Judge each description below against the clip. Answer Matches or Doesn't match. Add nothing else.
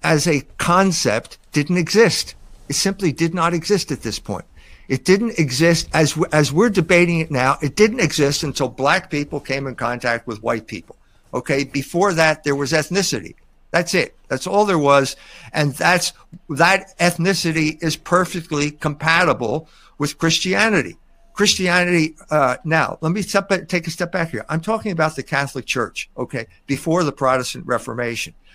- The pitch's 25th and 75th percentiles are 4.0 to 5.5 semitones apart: Matches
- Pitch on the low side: Doesn't match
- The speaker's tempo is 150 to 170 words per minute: Matches